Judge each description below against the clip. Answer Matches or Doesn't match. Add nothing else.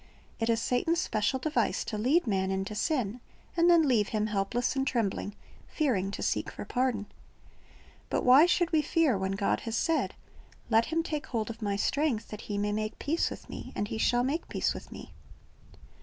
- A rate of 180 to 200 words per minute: Matches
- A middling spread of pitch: Doesn't match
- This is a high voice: Matches